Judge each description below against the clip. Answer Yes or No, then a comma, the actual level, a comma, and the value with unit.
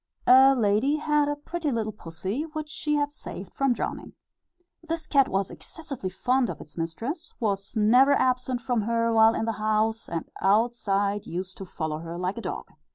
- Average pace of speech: Yes, average, 180 wpm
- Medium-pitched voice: No, high, 230 Hz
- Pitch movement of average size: No, wide, 5.8 semitones